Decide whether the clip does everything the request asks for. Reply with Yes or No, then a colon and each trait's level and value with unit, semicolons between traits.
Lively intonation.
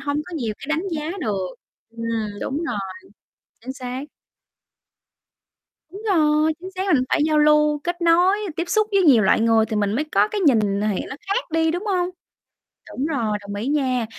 Yes: wide, 6.8 semitones